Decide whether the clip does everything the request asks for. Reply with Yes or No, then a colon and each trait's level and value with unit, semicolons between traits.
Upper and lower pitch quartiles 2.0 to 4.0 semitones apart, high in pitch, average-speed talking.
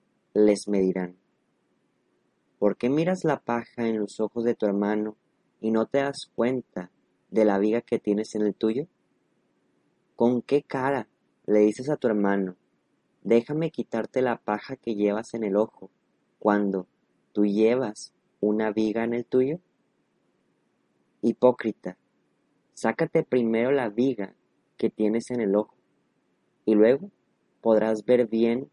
No: average, 2.9 semitones; low, 110 Hz; average, 140 wpm